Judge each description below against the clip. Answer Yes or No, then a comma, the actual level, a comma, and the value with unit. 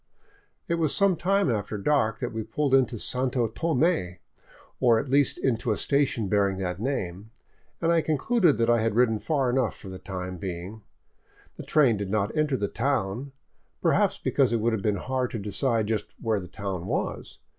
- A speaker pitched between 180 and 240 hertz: No, low, 115 Hz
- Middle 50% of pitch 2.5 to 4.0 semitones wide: No, average, 5.2 semitones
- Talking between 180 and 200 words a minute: Yes, average, 190 wpm